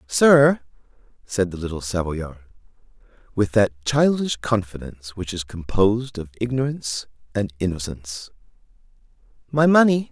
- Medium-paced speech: No, slow, 105 wpm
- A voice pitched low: Yes, low, 105 Hz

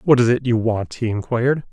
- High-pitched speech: No, low, 120 Hz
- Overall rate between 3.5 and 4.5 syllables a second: No, 5.6 syllables/s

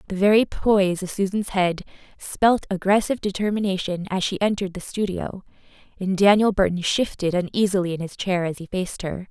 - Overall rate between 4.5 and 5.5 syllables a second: No, 5.7 syllables/s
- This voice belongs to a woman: Yes, female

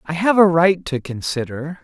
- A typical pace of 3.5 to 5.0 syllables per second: Yes, 4.7 syllables/s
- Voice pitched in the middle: Yes, medium, 165 Hz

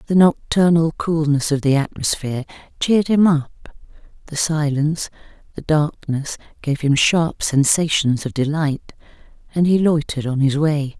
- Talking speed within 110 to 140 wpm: Yes, slow, 135 wpm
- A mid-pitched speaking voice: Yes, medium, 150 Hz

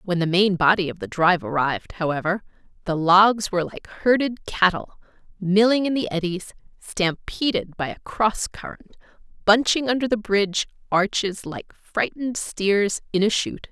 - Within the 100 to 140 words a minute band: No, average, 155 wpm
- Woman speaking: Yes, female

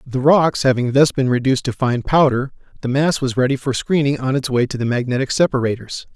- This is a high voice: No, low, 130 Hz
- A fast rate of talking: Yes, fast, 215 wpm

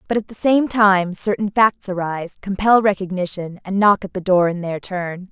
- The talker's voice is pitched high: Yes, high, 195 Hz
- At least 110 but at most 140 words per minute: No, fast, 205 wpm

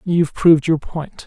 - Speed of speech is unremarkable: Yes, average, 190 wpm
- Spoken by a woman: No, male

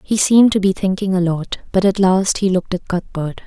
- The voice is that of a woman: Yes, female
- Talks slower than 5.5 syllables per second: No, 5.6 syllables/s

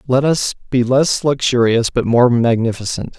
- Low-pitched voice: Yes, low, 125 Hz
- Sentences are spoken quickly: No, average, 150 wpm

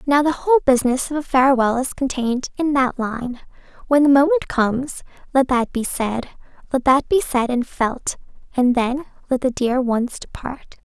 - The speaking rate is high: No, average, 180 wpm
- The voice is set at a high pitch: Yes, very high, 265 Hz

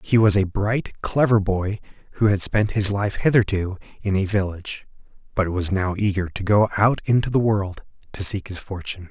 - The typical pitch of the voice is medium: No, low, 100 Hz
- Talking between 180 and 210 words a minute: Yes, average, 190 wpm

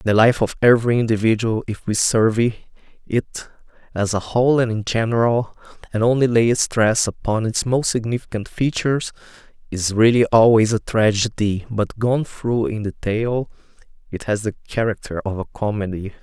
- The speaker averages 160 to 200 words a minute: No, average, 150 wpm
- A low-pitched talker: Yes, low, 110 Hz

